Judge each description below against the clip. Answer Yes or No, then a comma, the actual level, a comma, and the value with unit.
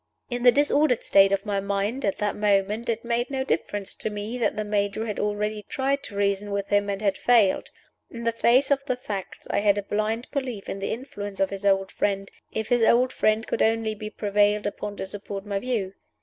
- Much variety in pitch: No, average, 2.7 semitones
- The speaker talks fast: Yes, fast, 225 wpm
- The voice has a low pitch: No, high, 210 Hz